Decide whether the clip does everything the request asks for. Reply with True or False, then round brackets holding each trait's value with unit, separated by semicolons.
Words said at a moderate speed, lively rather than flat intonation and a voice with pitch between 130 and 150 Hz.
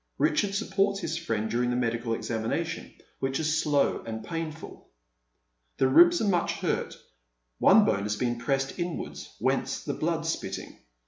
True (150 wpm; 6.6 semitones; 140 Hz)